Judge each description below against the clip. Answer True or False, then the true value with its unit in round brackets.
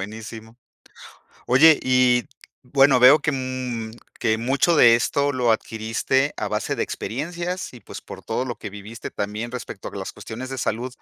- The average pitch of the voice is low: True (125 Hz)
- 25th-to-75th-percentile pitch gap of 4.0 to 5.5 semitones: False (3.1 semitones)